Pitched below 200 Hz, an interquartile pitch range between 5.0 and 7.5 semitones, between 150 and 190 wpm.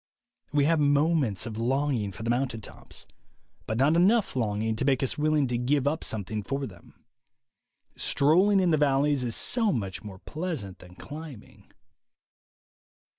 Yes: low, 135 Hz; wide, 5.5 semitones; average, 155 wpm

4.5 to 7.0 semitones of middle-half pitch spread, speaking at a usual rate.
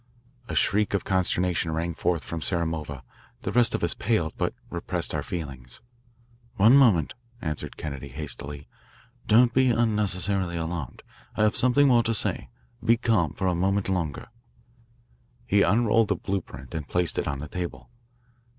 Yes: wide, 5.4 semitones; average, 160 wpm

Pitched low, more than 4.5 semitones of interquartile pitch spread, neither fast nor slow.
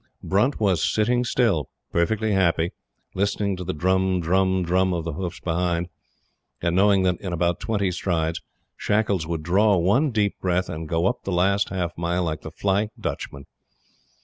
No: very low, 95 Hz; average, 2.7 semitones; average, 170 wpm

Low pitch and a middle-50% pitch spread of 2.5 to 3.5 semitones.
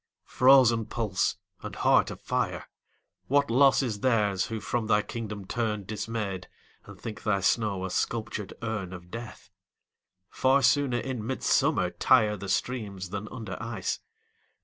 Yes: low, 110 Hz; average, 3.2 semitones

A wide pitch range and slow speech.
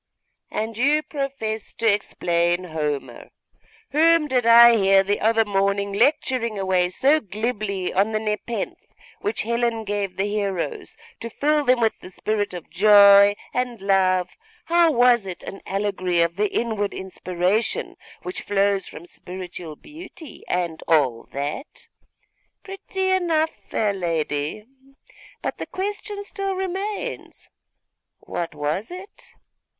Yes: wide, 6.1 semitones; slow, 130 wpm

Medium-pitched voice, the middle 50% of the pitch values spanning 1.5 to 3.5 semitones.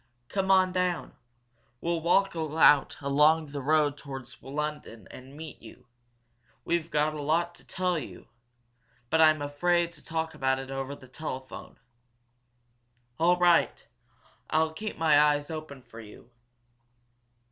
Yes: medium, 155 Hz; average, 3.1 semitones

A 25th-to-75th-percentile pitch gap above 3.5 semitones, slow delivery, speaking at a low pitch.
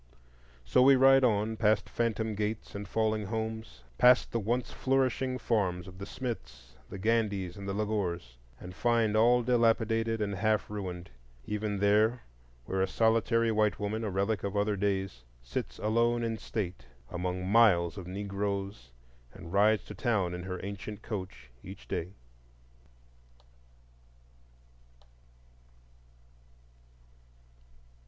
No: average, 3.1 semitones; slow, 125 wpm; low, 105 Hz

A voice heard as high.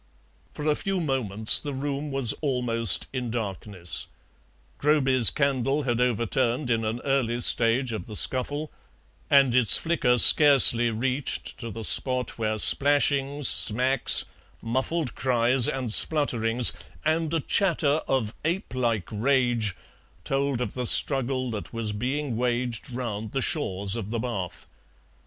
No: low, 125 Hz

